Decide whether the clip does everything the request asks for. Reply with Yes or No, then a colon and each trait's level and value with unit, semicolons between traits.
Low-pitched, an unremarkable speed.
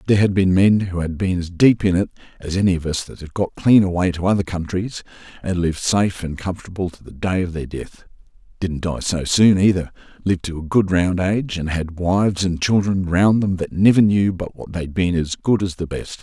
No: very low, 90 Hz; fast, 230 wpm